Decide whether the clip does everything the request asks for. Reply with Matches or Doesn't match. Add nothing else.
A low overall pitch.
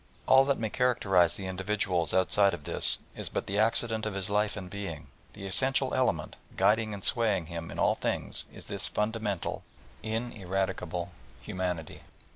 Matches